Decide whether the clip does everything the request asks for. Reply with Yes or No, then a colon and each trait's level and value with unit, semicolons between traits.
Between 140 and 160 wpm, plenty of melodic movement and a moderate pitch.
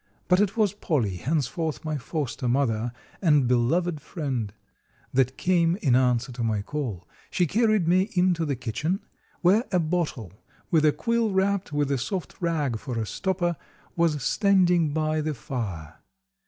Yes: average, 155 wpm; wide, 6.2 semitones; medium, 155 Hz